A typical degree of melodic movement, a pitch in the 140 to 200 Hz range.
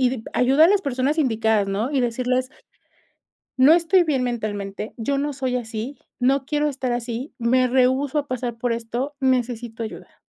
No: average, 3.1 semitones; very high, 255 Hz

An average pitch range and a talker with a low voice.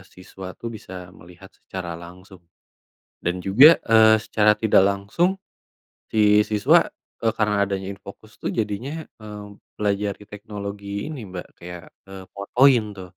No: narrow, 2.2 semitones; low, 100 Hz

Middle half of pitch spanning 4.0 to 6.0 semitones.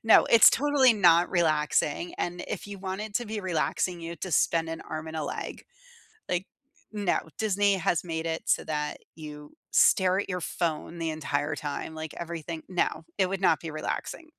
No: average, 3.3 semitones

